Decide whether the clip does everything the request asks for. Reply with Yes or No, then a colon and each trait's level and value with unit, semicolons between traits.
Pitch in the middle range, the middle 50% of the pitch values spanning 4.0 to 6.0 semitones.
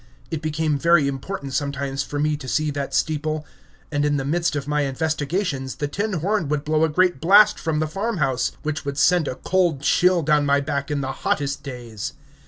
No: medium, 150 Hz; narrow, 2.5 semitones